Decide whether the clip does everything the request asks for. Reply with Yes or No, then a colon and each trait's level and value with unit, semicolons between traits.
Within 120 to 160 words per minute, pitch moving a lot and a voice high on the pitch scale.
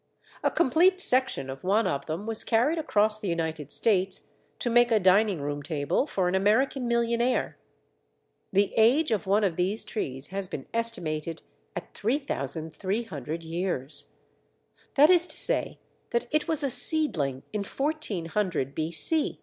Yes: average, 150 wpm; wide, 6.9 semitones; high, 200 Hz